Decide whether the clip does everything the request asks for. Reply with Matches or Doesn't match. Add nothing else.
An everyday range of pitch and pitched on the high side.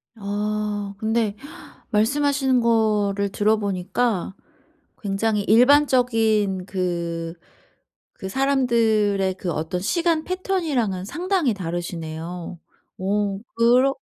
Matches